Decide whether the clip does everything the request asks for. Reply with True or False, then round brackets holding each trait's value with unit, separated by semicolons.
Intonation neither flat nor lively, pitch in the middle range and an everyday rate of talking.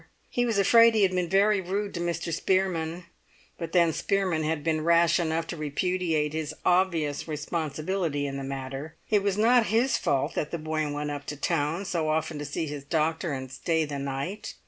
True (3.9 semitones; 165 Hz; 195 wpm)